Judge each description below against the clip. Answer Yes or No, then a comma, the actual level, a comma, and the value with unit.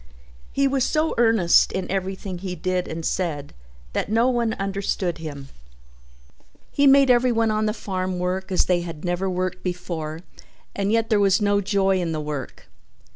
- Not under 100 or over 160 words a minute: No, average, 175 wpm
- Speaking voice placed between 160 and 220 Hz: Yes, high, 190 Hz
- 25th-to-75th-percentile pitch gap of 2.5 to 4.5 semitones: Yes, average, 3.6 semitones